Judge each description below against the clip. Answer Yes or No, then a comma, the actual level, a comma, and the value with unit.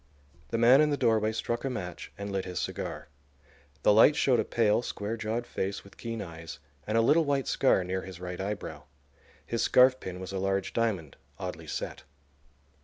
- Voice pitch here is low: Yes, low, 110 Hz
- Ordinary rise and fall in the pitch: Yes, average, 4.0 semitones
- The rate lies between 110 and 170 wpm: No, average, 185 wpm